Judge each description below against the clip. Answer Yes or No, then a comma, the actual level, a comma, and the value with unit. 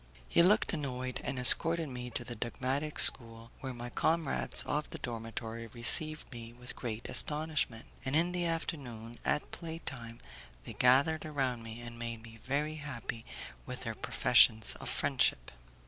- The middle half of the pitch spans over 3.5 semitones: Yes, average, 4.6 semitones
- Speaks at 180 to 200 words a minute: No, average, 160 wpm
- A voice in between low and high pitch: No, low, 125 Hz